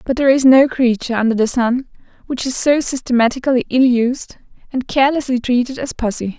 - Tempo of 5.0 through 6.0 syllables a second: Yes, 5.9 syllables/s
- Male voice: No, female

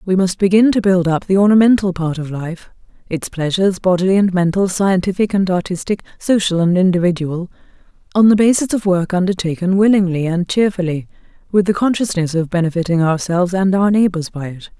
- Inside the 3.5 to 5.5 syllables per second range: No, 5.8 syllables/s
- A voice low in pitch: No, medium, 185 Hz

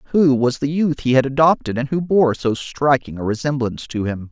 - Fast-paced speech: Yes, fast, 225 wpm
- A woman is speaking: No, male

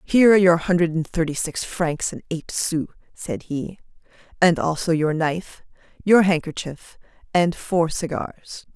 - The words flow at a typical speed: Yes, average, 150 wpm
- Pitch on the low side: No, medium, 170 Hz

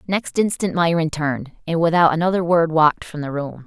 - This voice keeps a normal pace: Yes, average, 195 wpm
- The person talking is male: No, female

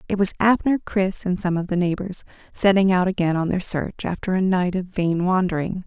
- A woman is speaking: Yes, female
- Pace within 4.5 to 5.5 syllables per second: Yes, 5.3 syllables/s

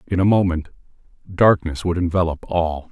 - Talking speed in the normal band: Yes, average, 145 wpm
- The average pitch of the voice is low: Yes, very low, 85 Hz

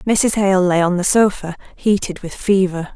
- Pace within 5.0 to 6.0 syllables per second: No, 4.5 syllables/s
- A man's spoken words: No, female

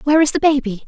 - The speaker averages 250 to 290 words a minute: Yes, fast, 275 wpm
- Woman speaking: Yes, female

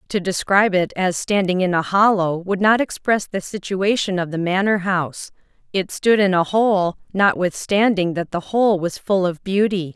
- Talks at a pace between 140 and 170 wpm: No, average, 180 wpm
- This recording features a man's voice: No, female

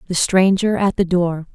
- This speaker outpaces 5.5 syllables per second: No, 4.6 syllables/s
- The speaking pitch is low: No, medium, 185 Hz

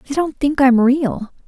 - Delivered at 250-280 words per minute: No, fast, 205 wpm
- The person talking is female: Yes, female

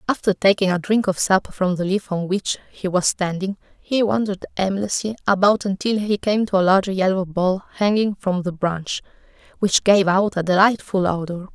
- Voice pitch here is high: Yes, high, 195 Hz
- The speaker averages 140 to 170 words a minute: No, average, 185 wpm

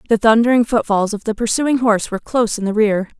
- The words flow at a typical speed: No, fast, 225 wpm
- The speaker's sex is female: Yes, female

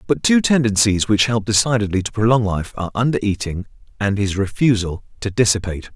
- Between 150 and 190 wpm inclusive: Yes, average, 170 wpm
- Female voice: No, male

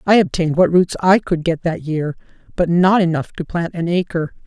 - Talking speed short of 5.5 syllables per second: Yes, 5.3 syllables/s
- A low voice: No, medium, 170 Hz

